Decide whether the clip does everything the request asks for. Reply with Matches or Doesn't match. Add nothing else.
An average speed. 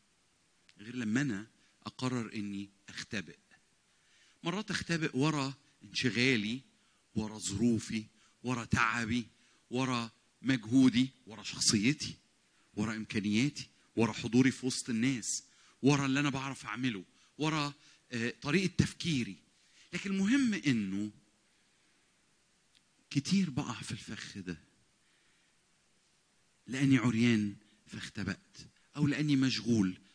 Doesn't match